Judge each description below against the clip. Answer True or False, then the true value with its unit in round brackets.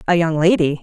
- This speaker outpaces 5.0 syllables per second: True (6.0 syllables/s)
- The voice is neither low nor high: True (165 Hz)